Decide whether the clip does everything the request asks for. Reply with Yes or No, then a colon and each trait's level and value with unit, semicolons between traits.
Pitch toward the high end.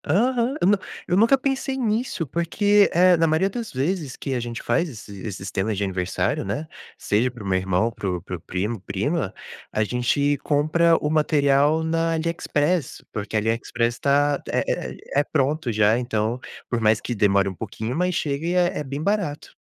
No: medium, 140 Hz